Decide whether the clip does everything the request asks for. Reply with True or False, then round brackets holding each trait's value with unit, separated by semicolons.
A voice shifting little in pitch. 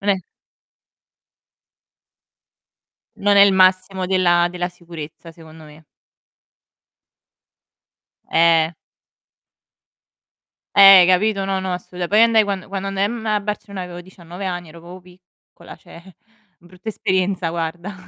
True (2.2 semitones)